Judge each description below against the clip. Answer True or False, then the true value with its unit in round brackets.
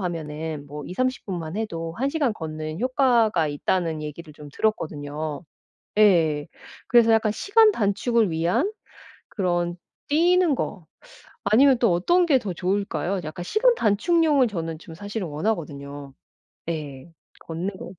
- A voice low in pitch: False (185 Hz)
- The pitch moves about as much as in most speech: False (6.9 semitones)